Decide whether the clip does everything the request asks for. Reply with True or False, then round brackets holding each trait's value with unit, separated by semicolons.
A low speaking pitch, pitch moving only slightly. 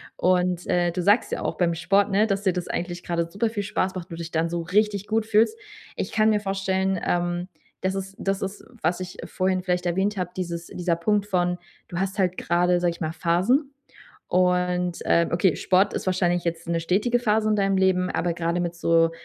False (180 Hz; 2.1 semitones)